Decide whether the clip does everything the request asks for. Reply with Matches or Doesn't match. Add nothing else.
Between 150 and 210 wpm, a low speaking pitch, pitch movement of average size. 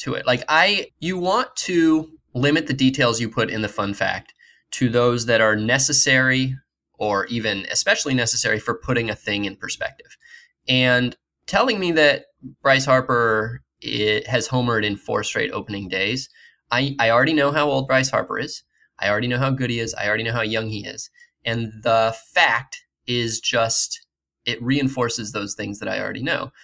Matches